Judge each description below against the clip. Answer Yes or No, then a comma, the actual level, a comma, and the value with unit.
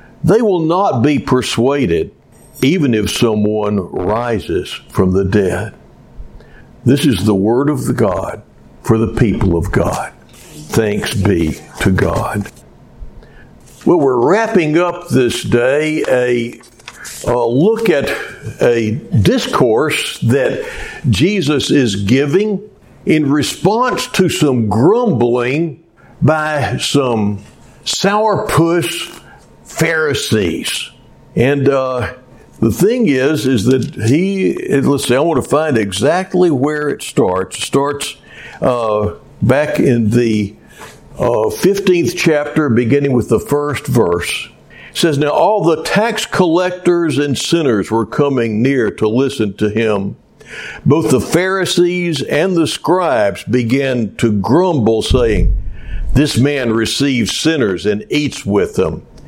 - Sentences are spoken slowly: Yes, slow, 120 wpm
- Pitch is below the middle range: Yes, low, 130 Hz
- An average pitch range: No, wide, 6.7 semitones